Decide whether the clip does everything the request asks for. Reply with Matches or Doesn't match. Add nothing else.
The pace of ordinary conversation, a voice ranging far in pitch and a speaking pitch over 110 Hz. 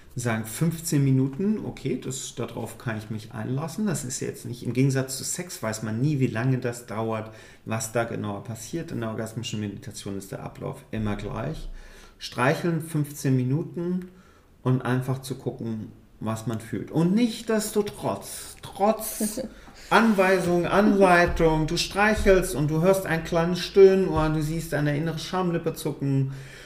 Matches